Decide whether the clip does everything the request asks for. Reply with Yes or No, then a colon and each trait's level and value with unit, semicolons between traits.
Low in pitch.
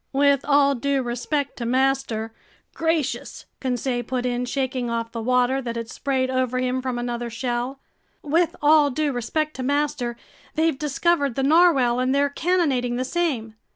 No: very high, 260 Hz